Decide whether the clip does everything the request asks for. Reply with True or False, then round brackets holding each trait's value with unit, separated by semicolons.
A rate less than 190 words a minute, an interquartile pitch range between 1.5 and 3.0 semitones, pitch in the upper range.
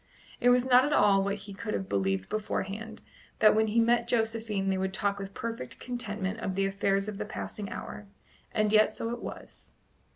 False (200 wpm; 2.6 semitones; 210 Hz)